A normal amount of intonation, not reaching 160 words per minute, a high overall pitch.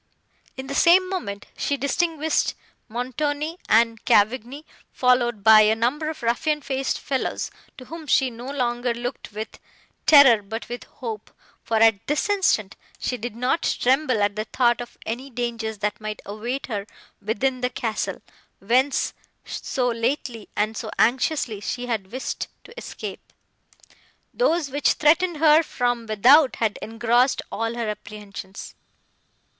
Yes: average, 4.0 semitones; average, 145 wpm; high, 245 Hz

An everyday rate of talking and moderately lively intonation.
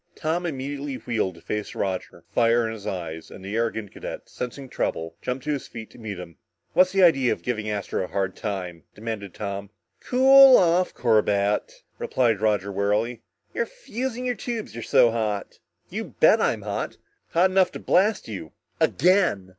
No: average, 175 wpm; wide, 9.0 semitones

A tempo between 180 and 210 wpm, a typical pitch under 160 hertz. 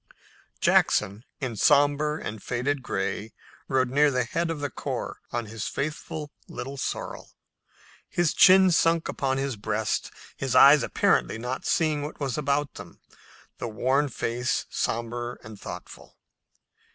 No: average, 140 wpm; low, 135 Hz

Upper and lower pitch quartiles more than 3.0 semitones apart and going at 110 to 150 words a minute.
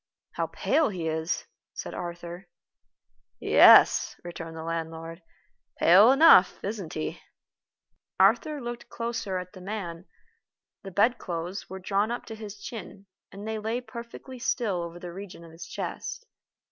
Yes: average, 4.8 semitones; average, 140 wpm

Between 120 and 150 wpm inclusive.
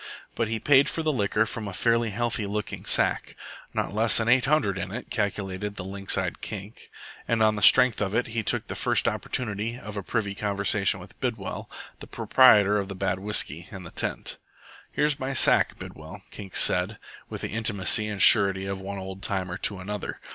No: average, 195 wpm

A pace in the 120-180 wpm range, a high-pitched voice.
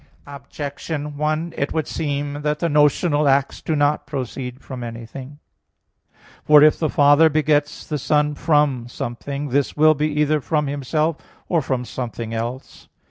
No: average, 150 wpm; medium, 145 Hz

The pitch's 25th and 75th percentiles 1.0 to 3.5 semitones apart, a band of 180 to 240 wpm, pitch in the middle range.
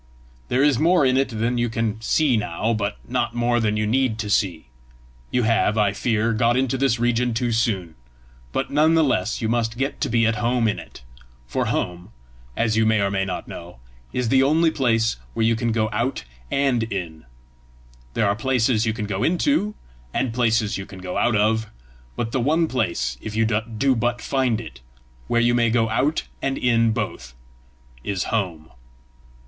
No: average, 2.8 semitones; average, 195 wpm; low, 115 Hz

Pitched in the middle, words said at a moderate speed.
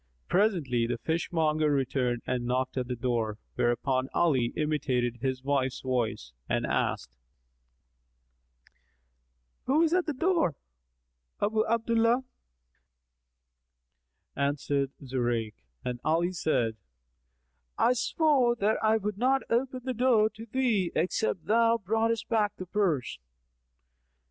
No: medium, 165 Hz; slow, 115 wpm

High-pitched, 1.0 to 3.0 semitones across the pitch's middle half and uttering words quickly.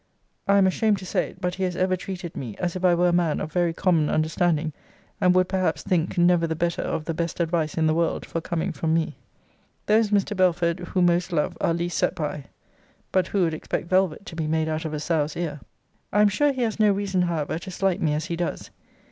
No: medium, 175 Hz; narrow, 2.5 semitones; fast, 240 wpm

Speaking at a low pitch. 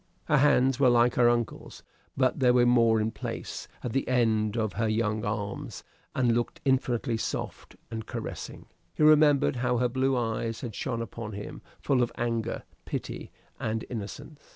Yes: low, 120 Hz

